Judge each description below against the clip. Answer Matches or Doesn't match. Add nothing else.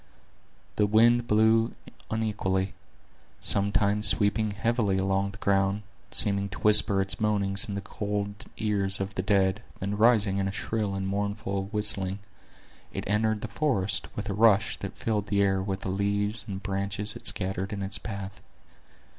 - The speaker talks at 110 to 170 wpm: Matches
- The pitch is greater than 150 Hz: Doesn't match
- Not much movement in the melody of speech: Matches